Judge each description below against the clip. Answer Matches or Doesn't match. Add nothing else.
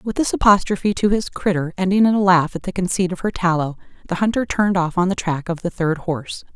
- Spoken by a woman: Matches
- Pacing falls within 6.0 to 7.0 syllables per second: Matches